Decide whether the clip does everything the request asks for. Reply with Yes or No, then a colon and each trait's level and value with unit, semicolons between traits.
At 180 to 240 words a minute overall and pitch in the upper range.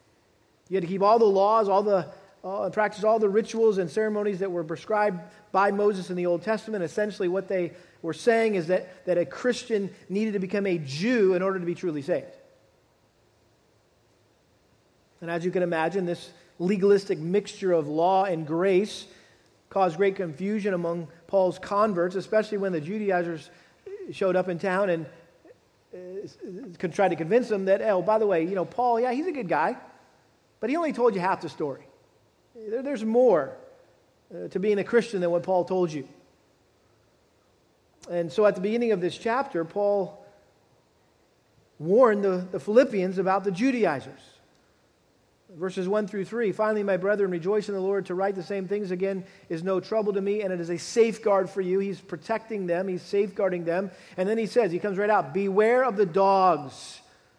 Yes: average, 185 wpm; high, 195 Hz